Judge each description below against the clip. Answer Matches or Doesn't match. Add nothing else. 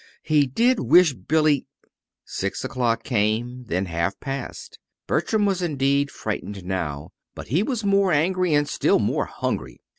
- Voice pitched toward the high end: Doesn't match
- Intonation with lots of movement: Matches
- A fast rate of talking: Doesn't match